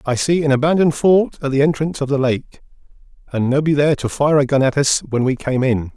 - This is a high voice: No, medium, 140 Hz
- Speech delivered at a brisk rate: Yes, fast, 240 wpm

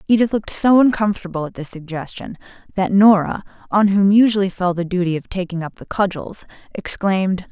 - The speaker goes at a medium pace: Yes, average, 170 wpm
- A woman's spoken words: Yes, female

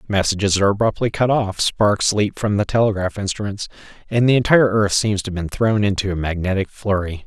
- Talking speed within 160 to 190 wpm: No, average, 200 wpm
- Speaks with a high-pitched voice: No, low, 100 Hz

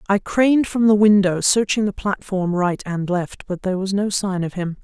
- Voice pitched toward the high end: Yes, high, 195 Hz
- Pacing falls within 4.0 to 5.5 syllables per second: Yes, 5.0 syllables/s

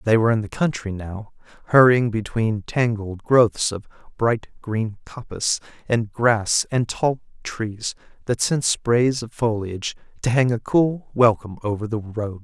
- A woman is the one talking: No, male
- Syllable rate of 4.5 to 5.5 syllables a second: No, 4.3 syllables/s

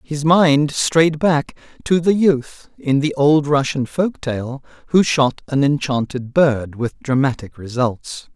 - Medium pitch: Yes, medium, 145 Hz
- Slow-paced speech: No, average, 150 wpm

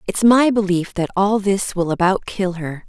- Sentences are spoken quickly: Yes, fast, 210 wpm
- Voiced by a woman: Yes, female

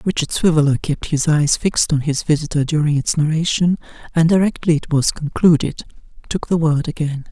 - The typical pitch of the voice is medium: Yes, medium, 155 Hz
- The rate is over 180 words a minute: No, average, 170 wpm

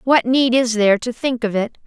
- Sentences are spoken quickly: Yes, fast, 260 wpm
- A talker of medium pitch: No, high, 240 Hz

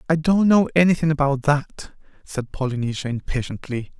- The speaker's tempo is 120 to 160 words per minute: Yes, slow, 135 wpm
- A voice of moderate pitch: Yes, medium, 145 Hz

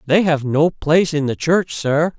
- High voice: No, medium, 155 Hz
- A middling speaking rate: No, fast, 220 wpm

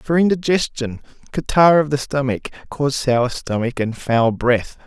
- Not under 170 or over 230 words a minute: No, average, 150 wpm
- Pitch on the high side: No, low, 135 Hz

